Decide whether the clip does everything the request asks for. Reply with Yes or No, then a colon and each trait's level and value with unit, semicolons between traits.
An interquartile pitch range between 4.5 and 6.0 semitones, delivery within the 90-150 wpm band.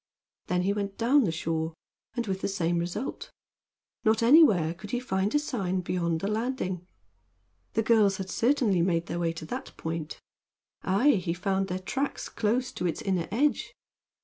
No: average, 4.8 semitones; average, 175 wpm